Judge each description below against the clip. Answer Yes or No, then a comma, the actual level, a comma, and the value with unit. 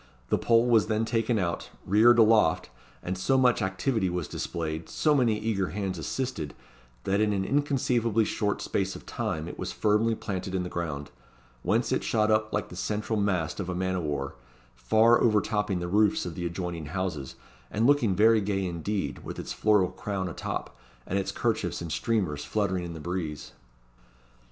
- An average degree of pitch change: Yes, average, 4.0 semitones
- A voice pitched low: Yes, low, 100 Hz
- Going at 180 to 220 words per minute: Yes, average, 185 wpm